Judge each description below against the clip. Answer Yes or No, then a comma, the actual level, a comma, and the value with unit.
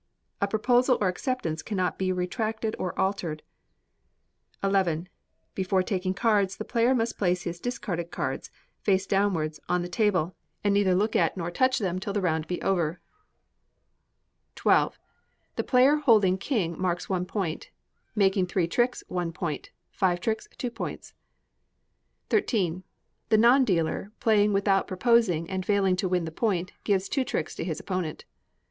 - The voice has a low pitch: No, high, 190 Hz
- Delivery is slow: No, average, 155 wpm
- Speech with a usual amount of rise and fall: Yes, average, 3.5 semitones